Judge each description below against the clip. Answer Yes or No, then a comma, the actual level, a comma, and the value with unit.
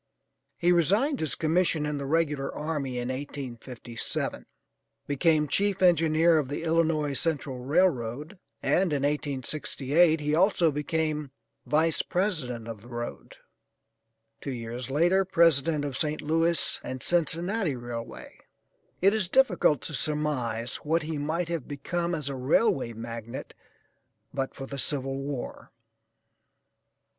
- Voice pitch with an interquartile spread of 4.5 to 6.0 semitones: No, average, 3.9 semitones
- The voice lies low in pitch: No, medium, 150 Hz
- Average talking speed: No, slow, 130 wpm